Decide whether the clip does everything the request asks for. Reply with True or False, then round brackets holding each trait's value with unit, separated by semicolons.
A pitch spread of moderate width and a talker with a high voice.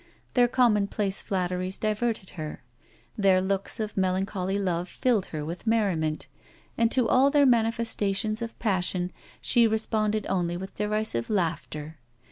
True (3.5 semitones; 200 Hz)